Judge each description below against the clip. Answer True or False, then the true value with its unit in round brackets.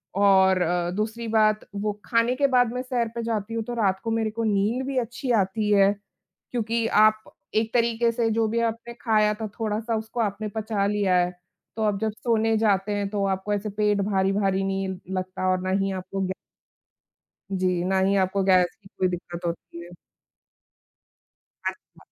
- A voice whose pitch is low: False (210 Hz)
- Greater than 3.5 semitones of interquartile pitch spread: False (2.8 semitones)